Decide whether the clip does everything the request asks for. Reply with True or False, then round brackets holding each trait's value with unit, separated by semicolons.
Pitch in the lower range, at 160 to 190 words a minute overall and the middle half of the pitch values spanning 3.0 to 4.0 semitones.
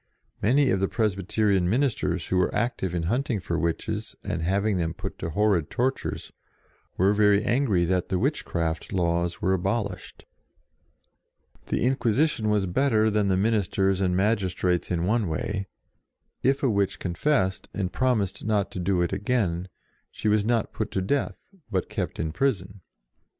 True (100 Hz; 165 wpm; 3.4 semitones)